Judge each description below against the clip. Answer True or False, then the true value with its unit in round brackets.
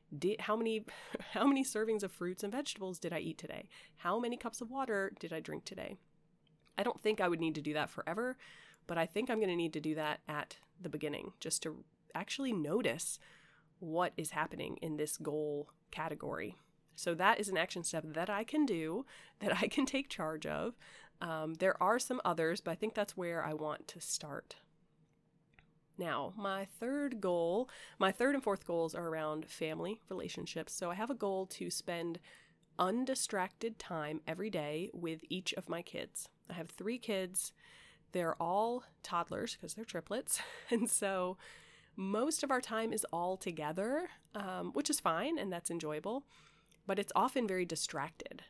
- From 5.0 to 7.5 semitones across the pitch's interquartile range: True (5.4 semitones)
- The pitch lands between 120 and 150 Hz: False (185 Hz)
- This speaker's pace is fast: False (180 wpm)